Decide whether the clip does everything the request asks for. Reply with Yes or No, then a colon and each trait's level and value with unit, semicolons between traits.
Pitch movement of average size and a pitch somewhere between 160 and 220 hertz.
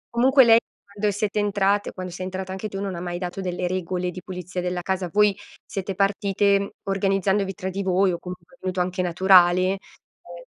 No: narrow, 1.7 semitones; high, 190 Hz